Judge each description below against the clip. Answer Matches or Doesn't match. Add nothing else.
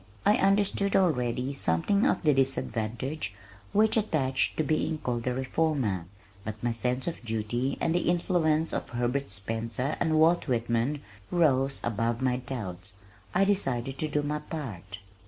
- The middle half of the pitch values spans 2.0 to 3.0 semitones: Doesn't match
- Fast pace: Doesn't match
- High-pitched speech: Doesn't match